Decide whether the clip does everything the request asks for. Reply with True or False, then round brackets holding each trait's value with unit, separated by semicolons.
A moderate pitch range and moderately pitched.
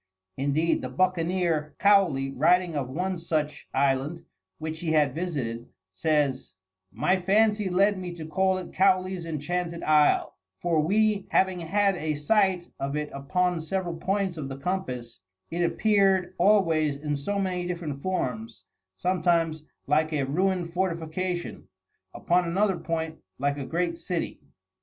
True (3.8 semitones; 170 Hz)